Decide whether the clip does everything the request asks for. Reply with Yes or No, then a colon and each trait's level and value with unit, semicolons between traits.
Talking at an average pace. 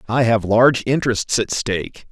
Yes: average, 170 wpm